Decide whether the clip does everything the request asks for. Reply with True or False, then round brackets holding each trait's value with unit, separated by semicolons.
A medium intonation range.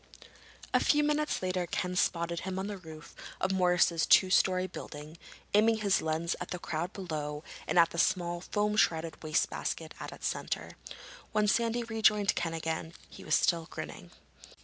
True (3.7 semitones)